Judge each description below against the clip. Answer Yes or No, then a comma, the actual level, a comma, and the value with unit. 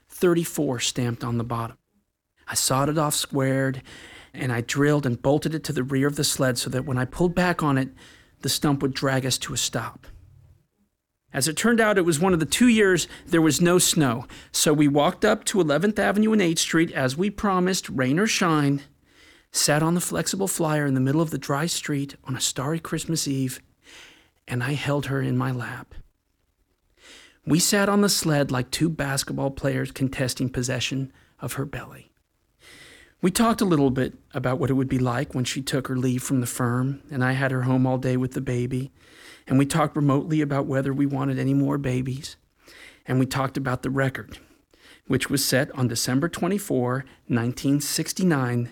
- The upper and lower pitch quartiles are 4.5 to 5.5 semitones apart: No, average, 3.6 semitones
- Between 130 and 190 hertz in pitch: Yes, medium, 140 Hz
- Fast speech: No, average, 195 wpm